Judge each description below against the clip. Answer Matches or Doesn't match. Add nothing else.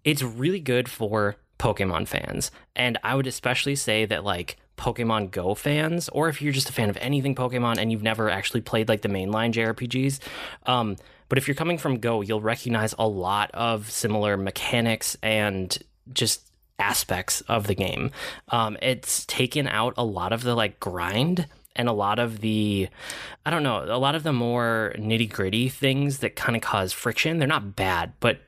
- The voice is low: Matches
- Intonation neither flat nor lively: Matches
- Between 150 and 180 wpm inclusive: Doesn't match